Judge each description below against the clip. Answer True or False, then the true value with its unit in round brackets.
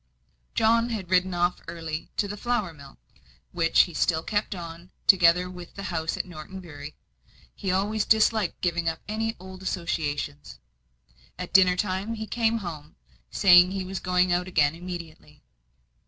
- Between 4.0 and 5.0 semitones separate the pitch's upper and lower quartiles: False (3.0 semitones)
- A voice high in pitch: False (180 Hz)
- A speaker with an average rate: True (155 wpm)